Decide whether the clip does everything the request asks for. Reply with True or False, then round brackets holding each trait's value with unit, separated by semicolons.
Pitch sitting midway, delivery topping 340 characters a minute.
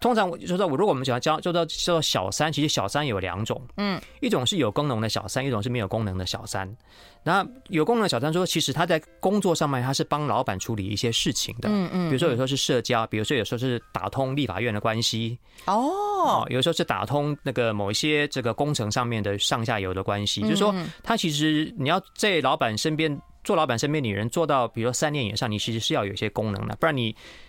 False (130 Hz; 365 characters per minute)